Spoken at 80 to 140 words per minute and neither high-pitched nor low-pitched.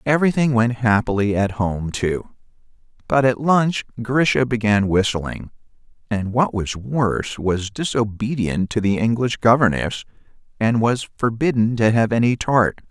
No: slow, 135 wpm; low, 115 Hz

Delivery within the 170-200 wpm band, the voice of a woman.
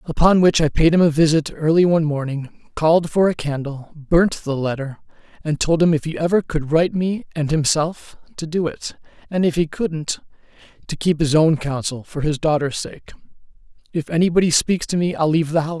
No: average, 195 wpm; male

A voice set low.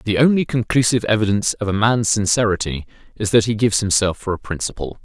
Yes: low, 110 Hz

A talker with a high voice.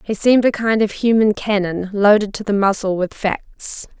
Yes: high, 205 Hz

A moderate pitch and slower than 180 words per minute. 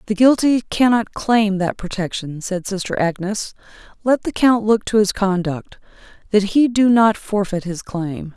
No: high, 205 Hz; average, 165 wpm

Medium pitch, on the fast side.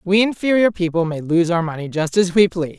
Yes: medium, 180 Hz; fast, 235 wpm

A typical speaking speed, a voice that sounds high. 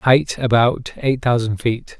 No: average, 150 wpm; low, 120 Hz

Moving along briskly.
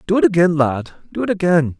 Yes: fast, 235 wpm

